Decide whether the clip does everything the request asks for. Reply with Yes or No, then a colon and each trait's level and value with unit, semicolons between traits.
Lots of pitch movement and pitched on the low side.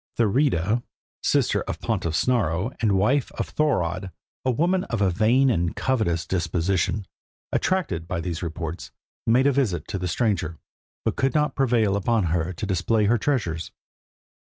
Yes: wide, 6.4 semitones; low, 100 Hz